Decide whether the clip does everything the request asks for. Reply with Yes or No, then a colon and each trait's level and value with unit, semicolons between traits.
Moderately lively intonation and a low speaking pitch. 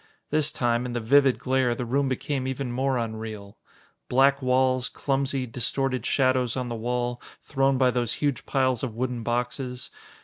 No: narrow, 1.9 semitones; low, 125 Hz